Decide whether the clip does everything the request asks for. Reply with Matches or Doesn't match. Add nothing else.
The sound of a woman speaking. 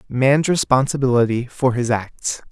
Doesn't match